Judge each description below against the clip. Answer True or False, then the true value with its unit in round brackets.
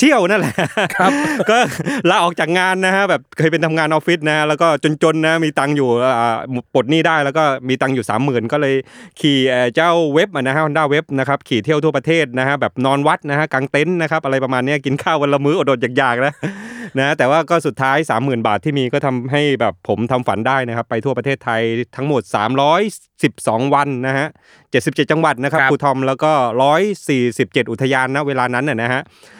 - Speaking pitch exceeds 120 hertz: True (140 Hz)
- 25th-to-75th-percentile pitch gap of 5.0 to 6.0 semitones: False (3.1 semitones)